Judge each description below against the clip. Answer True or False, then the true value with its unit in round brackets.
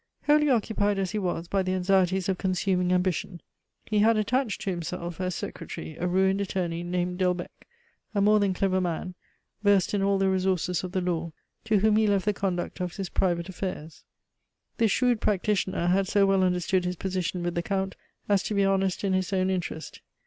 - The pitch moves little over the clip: True (1.9 semitones)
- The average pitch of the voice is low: False (190 Hz)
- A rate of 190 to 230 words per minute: True (195 wpm)